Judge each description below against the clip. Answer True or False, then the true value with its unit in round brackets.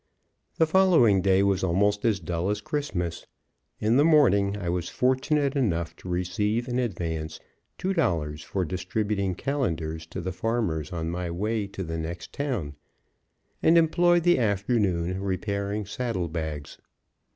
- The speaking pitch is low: True (100 Hz)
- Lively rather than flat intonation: True (5.9 semitones)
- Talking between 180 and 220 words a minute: False (145 wpm)